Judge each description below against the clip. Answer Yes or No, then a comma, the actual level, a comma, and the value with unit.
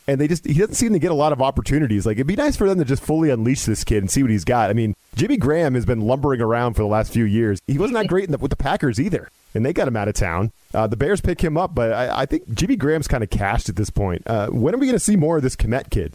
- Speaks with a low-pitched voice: Yes, low, 130 Hz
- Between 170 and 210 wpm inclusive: No, fast, 330 wpm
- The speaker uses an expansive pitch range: Yes, wide, 6.1 semitones